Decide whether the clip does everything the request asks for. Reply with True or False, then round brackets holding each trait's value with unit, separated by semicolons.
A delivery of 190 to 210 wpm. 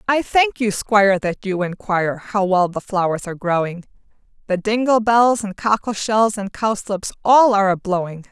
False (175 wpm)